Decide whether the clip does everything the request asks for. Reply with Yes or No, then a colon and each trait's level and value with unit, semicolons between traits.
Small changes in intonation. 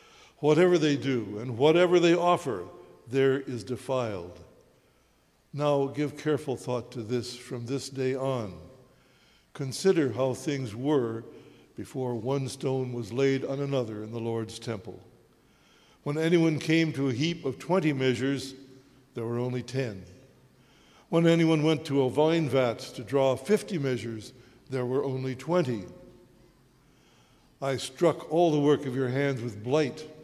No: average, 3.3 semitones